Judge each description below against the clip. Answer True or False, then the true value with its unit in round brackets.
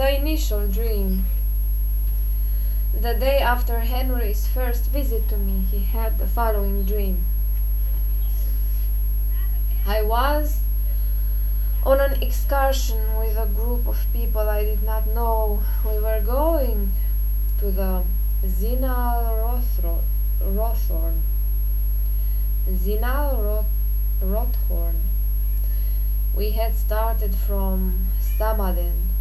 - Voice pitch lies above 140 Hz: True (190 Hz)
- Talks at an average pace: False (90 wpm)